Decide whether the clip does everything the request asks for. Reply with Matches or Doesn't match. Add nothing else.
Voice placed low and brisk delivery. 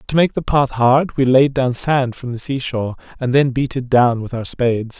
Matches